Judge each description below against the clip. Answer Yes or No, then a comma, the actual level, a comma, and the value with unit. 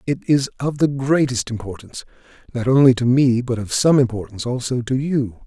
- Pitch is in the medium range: No, low, 125 Hz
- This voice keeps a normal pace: Yes, average, 185 wpm